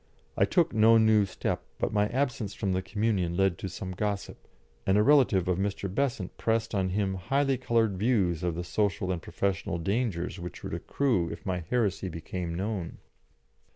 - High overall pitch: No, low, 100 Hz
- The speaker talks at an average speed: Yes, average, 180 wpm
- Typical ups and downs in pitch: Yes, average, 3.5 semitones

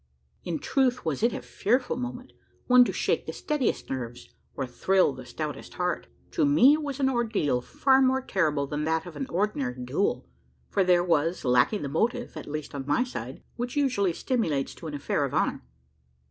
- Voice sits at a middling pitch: Yes, medium, 180 Hz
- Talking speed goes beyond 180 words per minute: Yes, average, 190 wpm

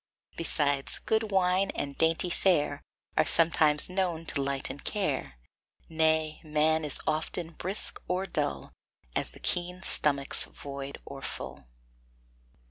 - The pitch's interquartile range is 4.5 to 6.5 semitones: No, average, 4.0 semitones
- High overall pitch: No, medium, 160 Hz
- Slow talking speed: Yes, slow, 125 wpm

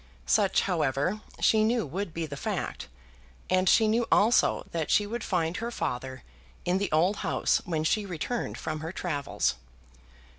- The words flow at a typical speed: Yes, average, 160 wpm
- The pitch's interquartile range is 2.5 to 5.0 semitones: No, wide, 5.4 semitones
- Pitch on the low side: No, medium, 180 Hz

